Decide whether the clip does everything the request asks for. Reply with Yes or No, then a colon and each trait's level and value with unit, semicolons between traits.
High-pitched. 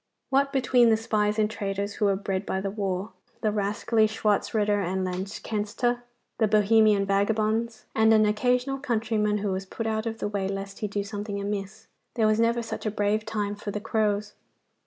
Yes: high, 210 Hz